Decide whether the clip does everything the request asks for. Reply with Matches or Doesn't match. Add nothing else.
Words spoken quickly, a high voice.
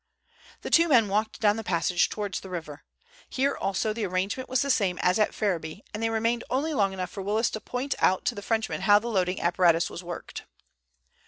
Matches